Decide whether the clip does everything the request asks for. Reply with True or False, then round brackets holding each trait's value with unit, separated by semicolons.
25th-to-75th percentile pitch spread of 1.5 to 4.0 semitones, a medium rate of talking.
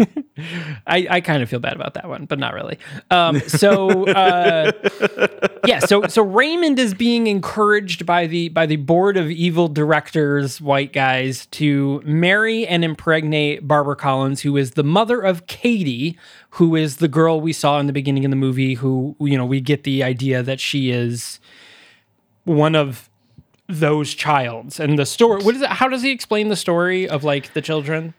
False (4.7 semitones; 185 wpm)